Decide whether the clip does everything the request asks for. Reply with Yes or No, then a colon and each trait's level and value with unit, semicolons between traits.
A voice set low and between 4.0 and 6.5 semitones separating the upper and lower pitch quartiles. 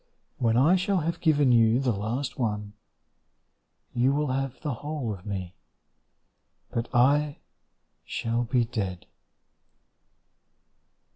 Yes: low, 125 Hz; average, 4.3 semitones